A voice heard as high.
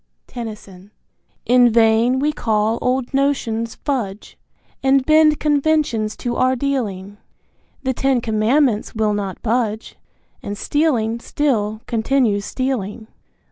Yes: high, 235 Hz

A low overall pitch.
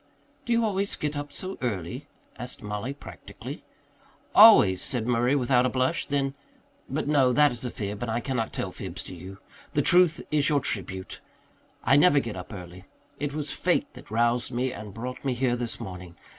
Yes: low, 125 Hz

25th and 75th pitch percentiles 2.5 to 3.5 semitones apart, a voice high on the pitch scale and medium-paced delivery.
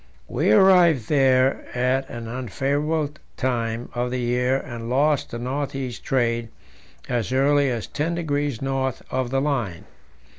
No: average, 2.9 semitones; low, 130 Hz; average, 145 wpm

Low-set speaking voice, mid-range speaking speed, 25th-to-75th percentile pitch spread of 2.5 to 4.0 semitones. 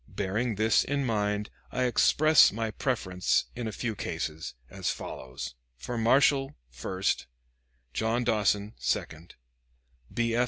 No: low, 110 Hz; slow, 125 wpm; average, 3.7 semitones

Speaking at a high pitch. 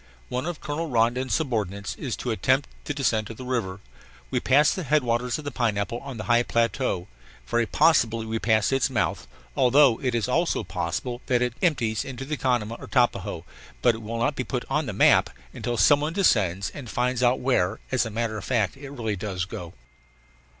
No: low, 120 Hz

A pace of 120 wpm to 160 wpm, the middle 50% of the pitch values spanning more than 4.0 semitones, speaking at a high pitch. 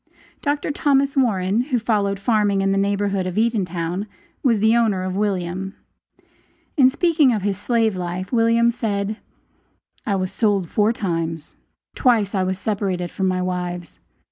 No: average, 150 wpm; average, 3.7 semitones; high, 200 Hz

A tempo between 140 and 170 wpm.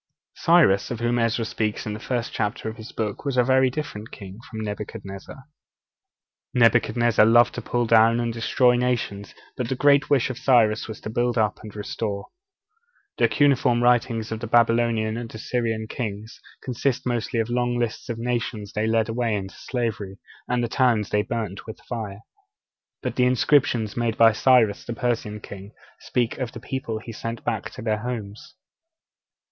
No: average, 180 wpm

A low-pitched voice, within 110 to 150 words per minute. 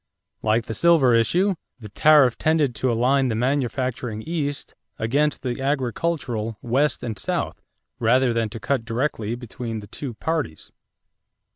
Yes: low, 125 Hz; average, 140 wpm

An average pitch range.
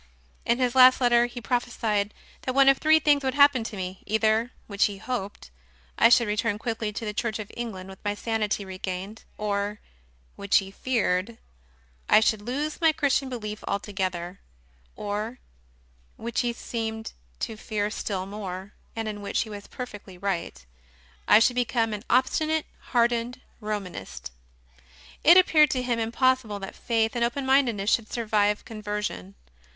Yes: average, 3.2 semitones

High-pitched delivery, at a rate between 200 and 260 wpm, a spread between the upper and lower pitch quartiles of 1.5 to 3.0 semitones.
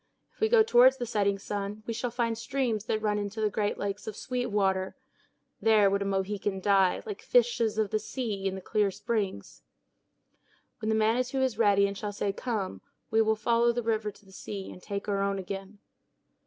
Yes: high, 210 Hz; fast, 205 wpm; average, 2.7 semitones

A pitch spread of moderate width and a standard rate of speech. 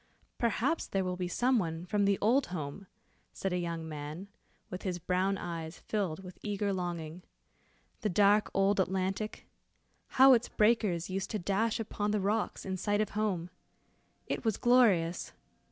Yes: average, 3.1 semitones; average, 160 wpm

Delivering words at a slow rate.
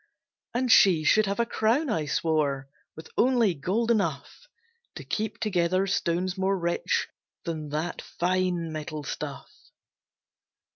Yes: slow, 130 wpm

